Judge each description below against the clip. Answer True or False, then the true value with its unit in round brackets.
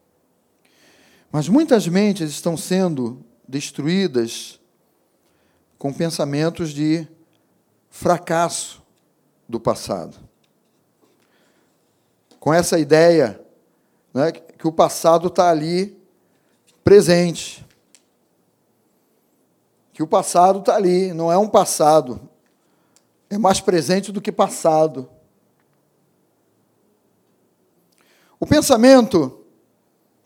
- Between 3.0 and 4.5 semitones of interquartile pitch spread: True (3.4 semitones)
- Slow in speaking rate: True (75 wpm)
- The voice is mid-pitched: True (170 Hz)